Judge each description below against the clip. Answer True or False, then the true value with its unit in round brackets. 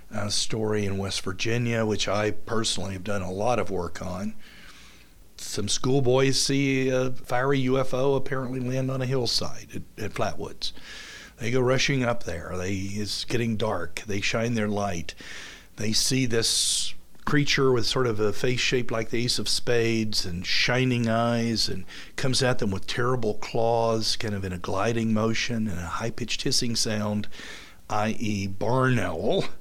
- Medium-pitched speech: False (115 Hz)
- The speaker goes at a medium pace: True (165 wpm)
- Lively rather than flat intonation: False (3.7 semitones)